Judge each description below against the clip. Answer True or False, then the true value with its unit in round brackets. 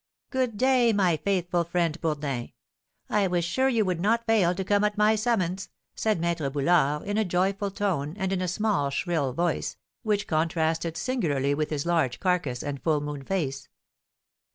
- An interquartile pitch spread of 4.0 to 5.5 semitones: True (5.0 semitones)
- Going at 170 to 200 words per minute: True (175 wpm)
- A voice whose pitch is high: False (175 Hz)